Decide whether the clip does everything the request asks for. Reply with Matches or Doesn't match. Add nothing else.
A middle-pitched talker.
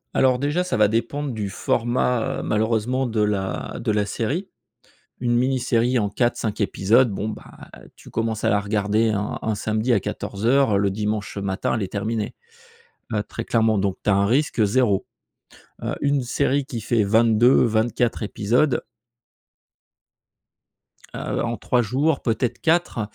Doesn't match